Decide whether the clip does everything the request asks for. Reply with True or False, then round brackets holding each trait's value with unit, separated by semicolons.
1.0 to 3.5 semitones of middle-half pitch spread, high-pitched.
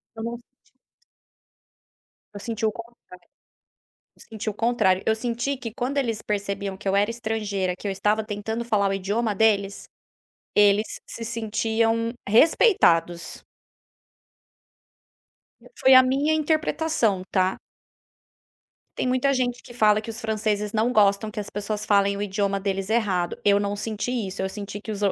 True (2.6 semitones; 215 Hz)